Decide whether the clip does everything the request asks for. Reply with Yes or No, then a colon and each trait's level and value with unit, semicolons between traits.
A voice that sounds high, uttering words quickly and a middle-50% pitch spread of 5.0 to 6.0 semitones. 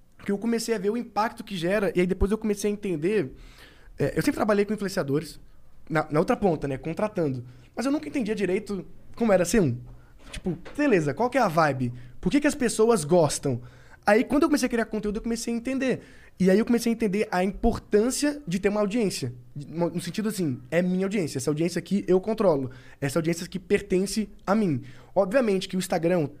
Yes: high, 195 Hz; fast, 215 wpm; average, 5.3 semitones